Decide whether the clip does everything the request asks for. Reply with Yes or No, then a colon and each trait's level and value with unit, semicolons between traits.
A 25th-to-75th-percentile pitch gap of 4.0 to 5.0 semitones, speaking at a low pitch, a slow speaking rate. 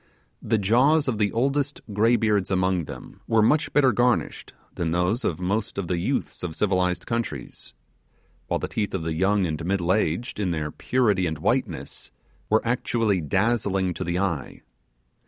No: average, 4.7 semitones; low, 100 Hz; average, 165 wpm